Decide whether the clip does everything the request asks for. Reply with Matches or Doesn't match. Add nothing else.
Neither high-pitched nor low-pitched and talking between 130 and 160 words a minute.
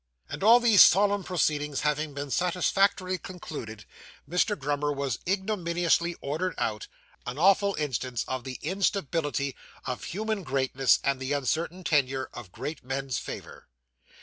Matches